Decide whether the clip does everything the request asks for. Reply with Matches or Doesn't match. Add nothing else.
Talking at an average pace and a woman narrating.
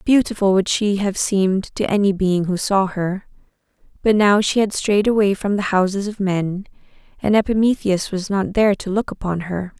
Matches